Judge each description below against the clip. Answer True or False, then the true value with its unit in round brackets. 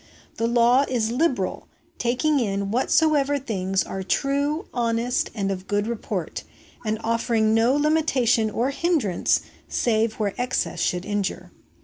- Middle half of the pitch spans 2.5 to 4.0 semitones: False (4.7 semitones)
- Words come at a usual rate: False (130 wpm)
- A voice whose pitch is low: False (235 Hz)